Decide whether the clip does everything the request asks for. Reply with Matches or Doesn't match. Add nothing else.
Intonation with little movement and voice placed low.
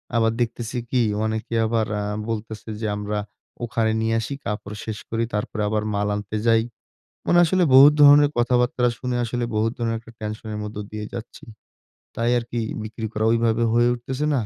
Matches